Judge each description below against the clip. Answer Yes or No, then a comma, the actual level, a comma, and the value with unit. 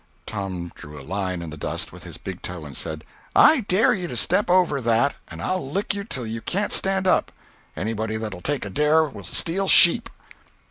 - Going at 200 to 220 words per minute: Yes, fast, 205 wpm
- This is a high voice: No, low, 120 Hz